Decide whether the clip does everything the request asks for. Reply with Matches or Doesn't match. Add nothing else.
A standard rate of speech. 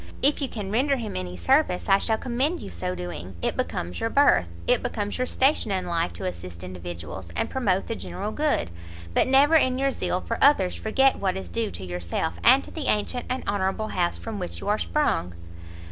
Doesn't match